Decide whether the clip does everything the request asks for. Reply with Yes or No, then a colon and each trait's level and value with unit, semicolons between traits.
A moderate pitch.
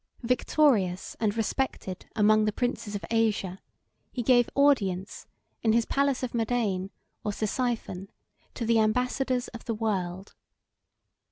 No: high, 225 Hz